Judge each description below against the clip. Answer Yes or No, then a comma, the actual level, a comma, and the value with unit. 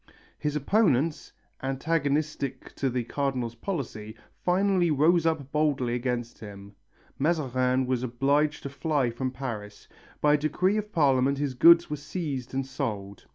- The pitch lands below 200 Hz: Yes, medium, 140 Hz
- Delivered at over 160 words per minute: No, average, 140 wpm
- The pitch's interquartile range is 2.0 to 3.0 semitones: No, average, 3.5 semitones